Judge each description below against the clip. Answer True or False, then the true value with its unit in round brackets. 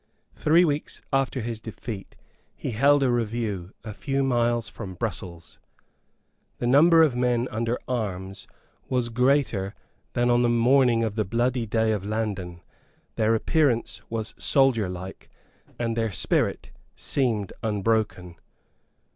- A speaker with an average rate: False (130 wpm)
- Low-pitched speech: True (115 Hz)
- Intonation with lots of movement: False (3.1 semitones)